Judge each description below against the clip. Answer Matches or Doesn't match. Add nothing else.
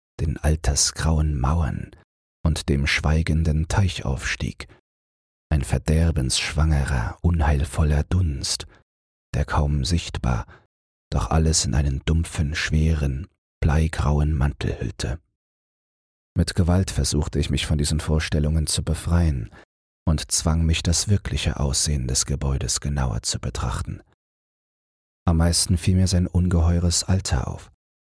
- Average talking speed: Doesn't match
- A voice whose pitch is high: Doesn't match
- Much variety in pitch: Doesn't match